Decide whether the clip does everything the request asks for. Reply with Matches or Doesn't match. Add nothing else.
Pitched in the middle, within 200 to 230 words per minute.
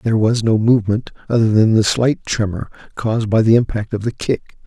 Doesn't match